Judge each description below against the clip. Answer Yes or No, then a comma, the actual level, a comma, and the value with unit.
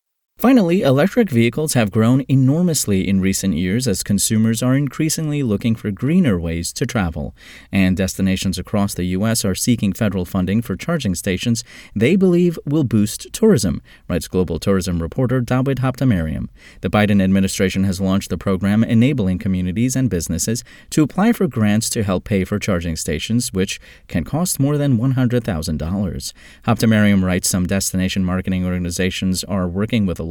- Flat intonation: No, average, 5.3 semitones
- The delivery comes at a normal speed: Yes, average, 155 wpm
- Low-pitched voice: Yes, low, 100 Hz